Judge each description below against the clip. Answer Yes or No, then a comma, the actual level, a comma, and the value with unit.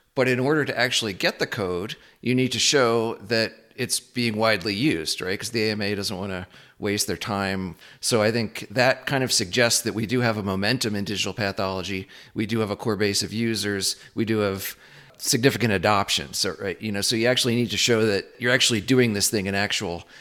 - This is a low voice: Yes, low, 110 Hz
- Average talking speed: No, fast, 220 wpm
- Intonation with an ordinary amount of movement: Yes, average, 3.0 semitones